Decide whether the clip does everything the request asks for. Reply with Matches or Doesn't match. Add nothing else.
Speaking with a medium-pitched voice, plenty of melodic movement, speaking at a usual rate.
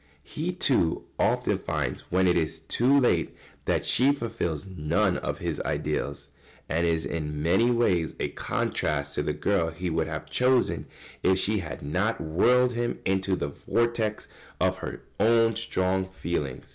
Doesn't match